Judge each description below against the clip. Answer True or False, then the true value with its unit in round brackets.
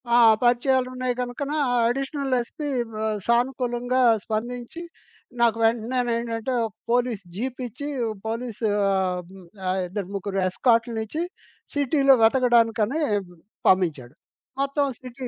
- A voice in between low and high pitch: False (240 Hz)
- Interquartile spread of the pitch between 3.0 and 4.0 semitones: False (2.6 semitones)